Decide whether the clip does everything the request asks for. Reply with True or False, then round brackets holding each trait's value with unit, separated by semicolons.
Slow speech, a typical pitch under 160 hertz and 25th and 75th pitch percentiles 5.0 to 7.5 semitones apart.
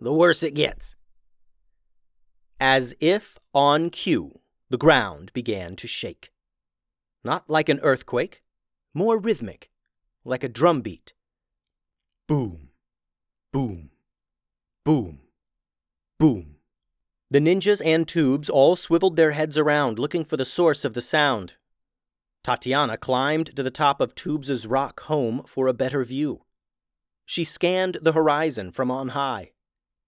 True (125 wpm; 140 Hz; 5.6 semitones)